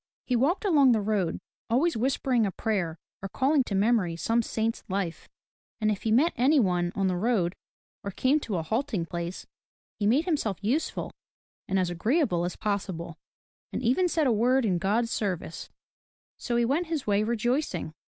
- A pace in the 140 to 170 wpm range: No, average, 180 wpm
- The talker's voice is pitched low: No, high, 220 Hz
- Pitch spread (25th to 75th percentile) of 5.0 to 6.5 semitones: Yes, wide, 5.5 semitones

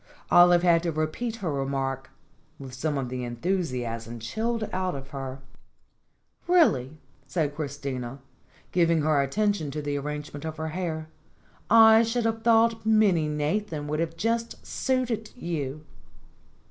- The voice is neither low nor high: Yes, medium, 155 Hz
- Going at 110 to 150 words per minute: Yes, slow, 135 wpm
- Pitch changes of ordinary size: No, wide, 7.4 semitones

